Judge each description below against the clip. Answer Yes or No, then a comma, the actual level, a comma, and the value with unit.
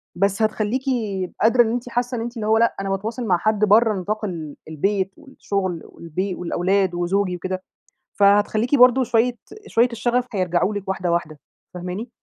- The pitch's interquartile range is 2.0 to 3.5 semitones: No, average, 4.1 semitones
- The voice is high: Yes, high, 205 Hz